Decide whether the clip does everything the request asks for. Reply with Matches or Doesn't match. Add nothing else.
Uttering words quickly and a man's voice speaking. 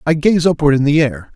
Matches